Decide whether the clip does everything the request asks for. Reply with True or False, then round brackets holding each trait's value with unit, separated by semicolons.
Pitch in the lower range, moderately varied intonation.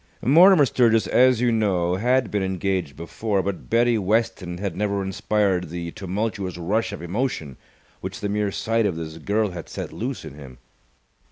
True (100 Hz; 4.1 semitones)